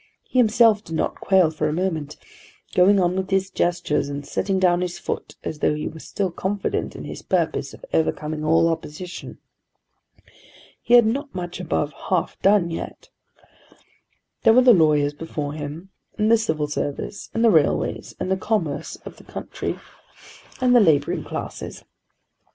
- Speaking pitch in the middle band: Yes, medium, 175 Hz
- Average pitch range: Yes, average, 4.7 semitones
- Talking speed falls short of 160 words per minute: No, average, 165 wpm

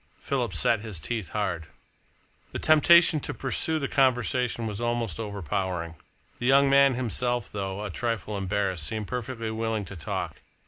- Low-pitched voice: Yes, low, 115 Hz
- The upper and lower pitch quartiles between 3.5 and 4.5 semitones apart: Yes, average, 4.0 semitones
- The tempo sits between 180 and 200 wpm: No, average, 150 wpm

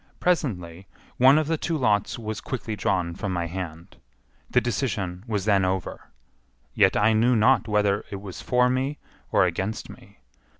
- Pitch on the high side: No, low, 105 Hz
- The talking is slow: No, average, 165 wpm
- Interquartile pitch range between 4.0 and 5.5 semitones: Yes, average, 4.8 semitones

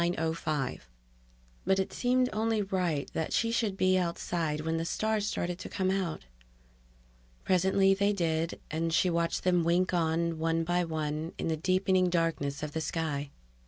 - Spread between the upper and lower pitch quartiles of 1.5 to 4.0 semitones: Yes, average, 2.8 semitones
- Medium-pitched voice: Yes, medium, 170 Hz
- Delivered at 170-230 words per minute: No, average, 160 wpm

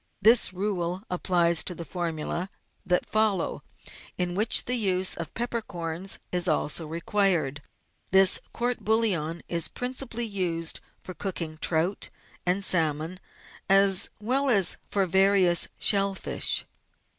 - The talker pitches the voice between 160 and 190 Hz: Yes, medium, 185 Hz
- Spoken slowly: Yes, slow, 125 wpm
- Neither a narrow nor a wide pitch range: Yes, average, 3.3 semitones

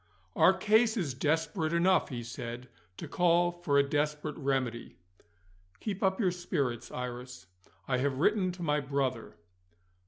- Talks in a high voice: No, medium, 150 Hz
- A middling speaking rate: Yes, average, 145 wpm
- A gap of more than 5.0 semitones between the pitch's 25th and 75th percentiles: Yes, wide, 5.6 semitones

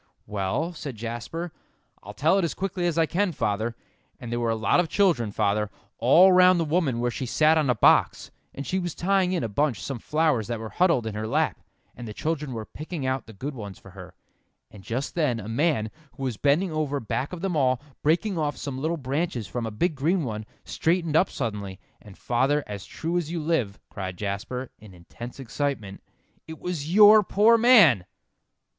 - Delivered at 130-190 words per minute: No, fast, 205 wpm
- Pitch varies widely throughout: Yes, wide, 7.1 semitones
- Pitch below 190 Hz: Yes, medium, 140 Hz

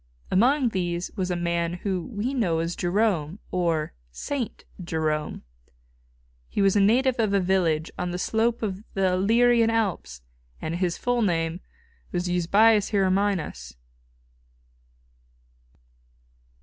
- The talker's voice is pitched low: No, medium, 185 Hz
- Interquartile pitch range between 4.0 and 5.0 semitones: Yes, average, 4.4 semitones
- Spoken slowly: Yes, slow, 125 wpm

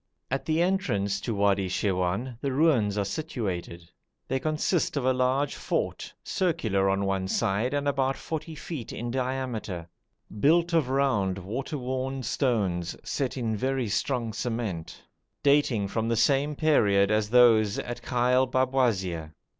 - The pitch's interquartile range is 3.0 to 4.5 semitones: No, wide, 5.4 semitones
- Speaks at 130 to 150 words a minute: Yes, average, 145 wpm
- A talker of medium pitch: No, low, 120 Hz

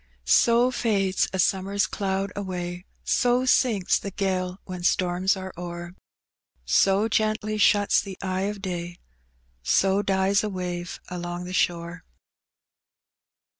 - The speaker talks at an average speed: No, slow, 125 wpm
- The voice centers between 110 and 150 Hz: No, high, 190 Hz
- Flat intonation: Yes, narrow, 2.2 semitones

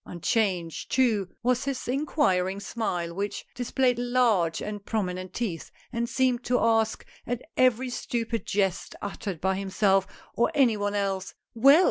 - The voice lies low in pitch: No, high, 220 Hz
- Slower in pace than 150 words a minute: Yes, average, 140 wpm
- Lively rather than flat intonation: No, average, 4.3 semitones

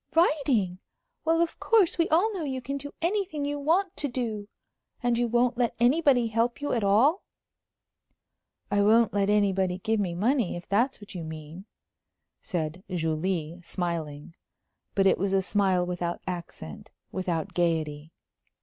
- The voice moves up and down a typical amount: No, wide, 7.6 semitones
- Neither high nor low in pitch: No, high, 205 Hz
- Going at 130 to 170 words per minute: Yes, average, 155 wpm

